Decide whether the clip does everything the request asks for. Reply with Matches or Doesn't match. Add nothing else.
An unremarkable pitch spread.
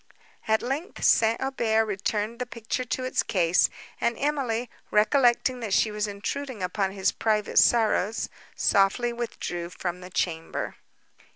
Matches